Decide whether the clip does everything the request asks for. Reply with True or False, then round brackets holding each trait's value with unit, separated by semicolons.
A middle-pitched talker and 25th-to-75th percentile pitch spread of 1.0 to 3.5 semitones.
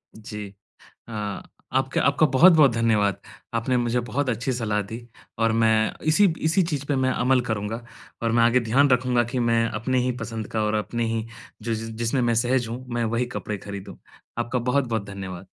False (115 Hz; 2.6 semitones)